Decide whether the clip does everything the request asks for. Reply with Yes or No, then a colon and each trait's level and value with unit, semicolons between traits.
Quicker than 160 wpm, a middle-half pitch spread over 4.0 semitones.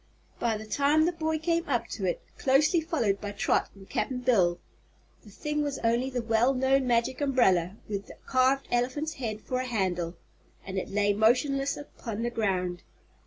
Yes: average, 180 wpm; average, 5.1 semitones